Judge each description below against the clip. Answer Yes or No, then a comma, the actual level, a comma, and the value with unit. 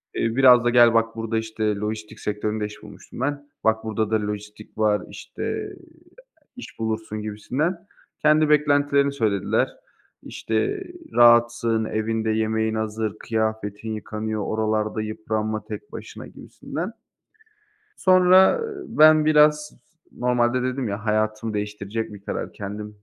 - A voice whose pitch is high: No, low, 110 Hz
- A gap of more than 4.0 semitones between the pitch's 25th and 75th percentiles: No, average, 2.9 semitones